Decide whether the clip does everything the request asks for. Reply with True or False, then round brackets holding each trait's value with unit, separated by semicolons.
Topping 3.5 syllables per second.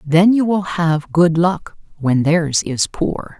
False (3.3 syllables/s)